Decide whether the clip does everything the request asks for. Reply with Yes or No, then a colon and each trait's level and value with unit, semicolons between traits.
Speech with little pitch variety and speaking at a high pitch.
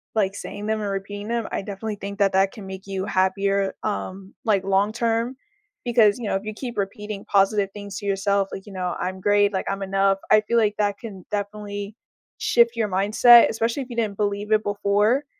Yes: narrow, 1.7 semitones; high, 205 Hz